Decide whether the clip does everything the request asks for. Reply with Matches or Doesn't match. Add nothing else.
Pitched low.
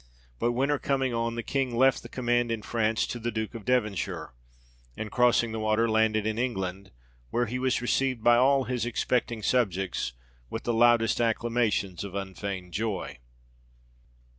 Matches